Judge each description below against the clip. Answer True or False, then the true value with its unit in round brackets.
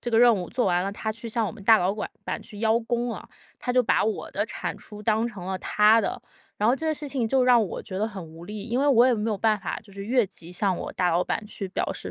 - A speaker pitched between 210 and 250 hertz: True (220 Hz)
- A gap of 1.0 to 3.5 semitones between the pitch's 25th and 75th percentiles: True (3.2 semitones)